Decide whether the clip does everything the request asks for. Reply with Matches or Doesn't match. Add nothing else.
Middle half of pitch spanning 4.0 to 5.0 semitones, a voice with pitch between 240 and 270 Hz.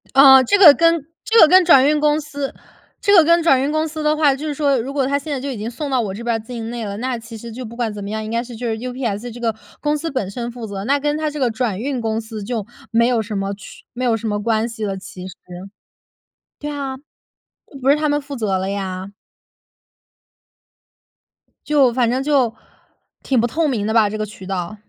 Matches